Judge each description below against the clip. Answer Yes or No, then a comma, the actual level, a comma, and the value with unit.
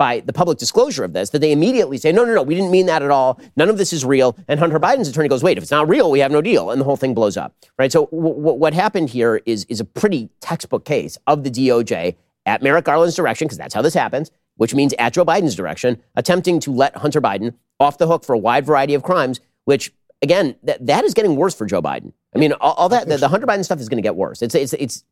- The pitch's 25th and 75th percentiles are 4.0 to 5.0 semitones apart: Yes, average, 4.3 semitones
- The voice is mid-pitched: Yes, medium, 145 Hz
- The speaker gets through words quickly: Yes, fast, 275 wpm